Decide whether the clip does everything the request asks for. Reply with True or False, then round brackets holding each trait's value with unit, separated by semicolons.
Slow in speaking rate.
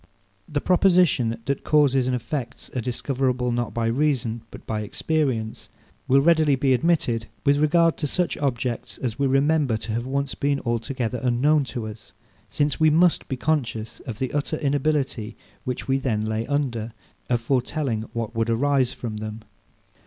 False (165 wpm)